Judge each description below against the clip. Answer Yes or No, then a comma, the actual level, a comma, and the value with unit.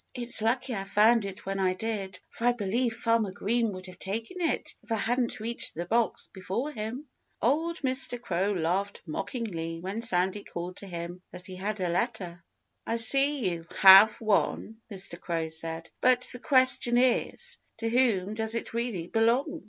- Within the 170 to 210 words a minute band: Yes, average, 175 wpm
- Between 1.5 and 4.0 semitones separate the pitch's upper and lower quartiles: No, average, 4.4 semitones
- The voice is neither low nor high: No, high, 215 Hz